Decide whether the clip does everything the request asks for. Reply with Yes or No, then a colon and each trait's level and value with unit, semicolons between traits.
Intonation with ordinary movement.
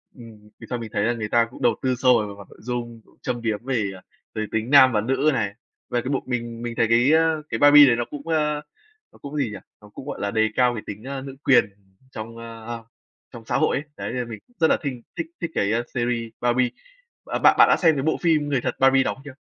Yes: average, 3.1 semitones